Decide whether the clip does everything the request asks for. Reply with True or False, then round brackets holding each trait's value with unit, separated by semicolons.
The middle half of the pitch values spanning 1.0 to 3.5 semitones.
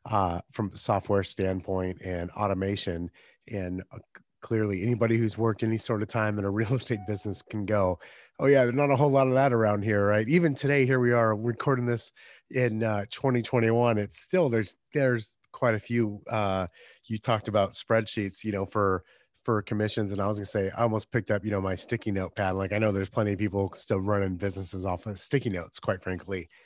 True (3.1 semitones)